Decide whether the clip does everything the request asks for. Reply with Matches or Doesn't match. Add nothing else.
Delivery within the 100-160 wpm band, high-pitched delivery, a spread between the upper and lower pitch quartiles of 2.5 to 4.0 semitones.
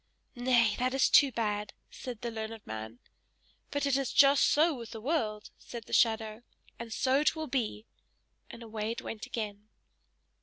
Doesn't match